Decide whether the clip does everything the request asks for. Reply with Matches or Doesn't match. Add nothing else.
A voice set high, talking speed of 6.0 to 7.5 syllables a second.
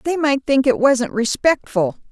Doesn't match